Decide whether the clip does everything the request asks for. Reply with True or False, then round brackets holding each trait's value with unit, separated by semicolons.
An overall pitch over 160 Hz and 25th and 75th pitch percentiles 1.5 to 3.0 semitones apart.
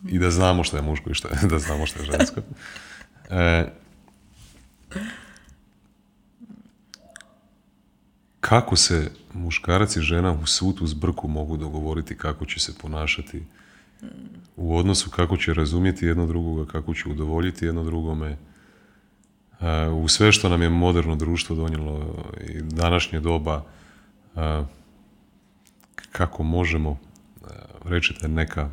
False (85 Hz; 2.6 semitones)